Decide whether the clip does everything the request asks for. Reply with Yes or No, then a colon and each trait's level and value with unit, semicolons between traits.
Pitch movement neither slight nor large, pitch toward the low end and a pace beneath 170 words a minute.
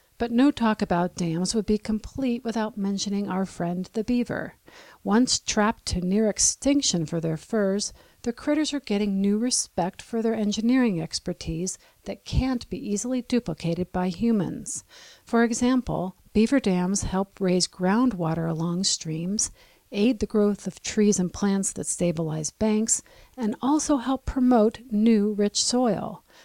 No: average, 4.4 semitones; high, 210 Hz; average, 145 wpm